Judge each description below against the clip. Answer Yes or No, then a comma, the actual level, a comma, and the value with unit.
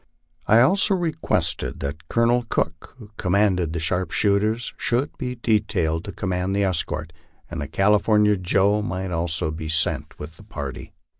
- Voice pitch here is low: Yes, very low, 95 Hz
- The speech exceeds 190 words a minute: No, average, 150 wpm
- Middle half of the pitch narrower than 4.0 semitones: No, average, 4.8 semitones